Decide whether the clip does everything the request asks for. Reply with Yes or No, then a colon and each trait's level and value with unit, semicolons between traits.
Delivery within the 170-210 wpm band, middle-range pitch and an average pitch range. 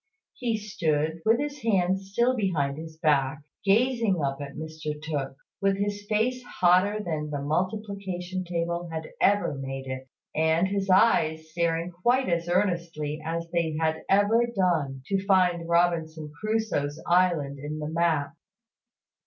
No: average, 145 wpm; medium, 170 Hz; average, 4.2 semitones